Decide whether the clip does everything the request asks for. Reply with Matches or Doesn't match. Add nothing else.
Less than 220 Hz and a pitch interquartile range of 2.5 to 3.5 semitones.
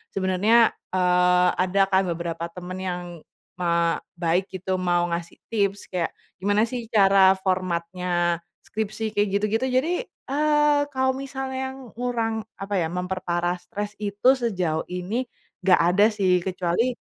Doesn't match